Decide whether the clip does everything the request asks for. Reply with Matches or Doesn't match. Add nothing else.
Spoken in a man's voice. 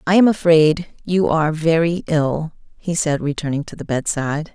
Doesn't match